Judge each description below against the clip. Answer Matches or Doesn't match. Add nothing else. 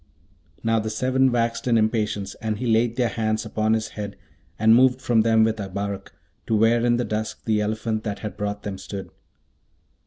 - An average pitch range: Doesn't match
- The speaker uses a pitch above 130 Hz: Doesn't match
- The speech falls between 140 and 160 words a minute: Doesn't match